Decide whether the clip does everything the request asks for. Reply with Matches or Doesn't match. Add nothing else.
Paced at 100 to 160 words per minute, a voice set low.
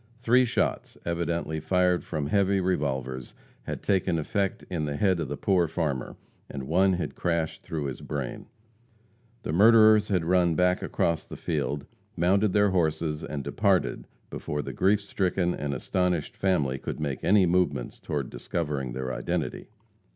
Matches